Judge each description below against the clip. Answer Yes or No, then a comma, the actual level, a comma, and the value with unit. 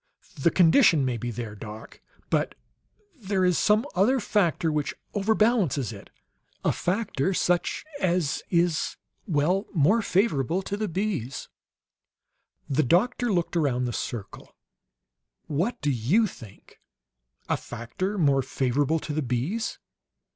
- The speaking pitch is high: No, medium, 165 Hz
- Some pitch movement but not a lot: No, wide, 6.9 semitones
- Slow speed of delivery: Yes, slow, 125 wpm